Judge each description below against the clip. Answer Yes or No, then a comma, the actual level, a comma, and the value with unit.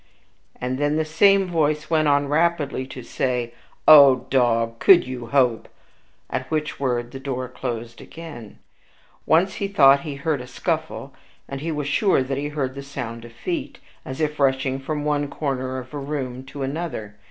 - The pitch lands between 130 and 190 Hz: Yes, medium, 140 Hz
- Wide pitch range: No, average, 3.1 semitones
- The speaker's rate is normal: Yes, average, 180 wpm